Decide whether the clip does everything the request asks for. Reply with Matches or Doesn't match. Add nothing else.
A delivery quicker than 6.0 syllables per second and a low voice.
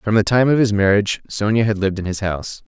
Matches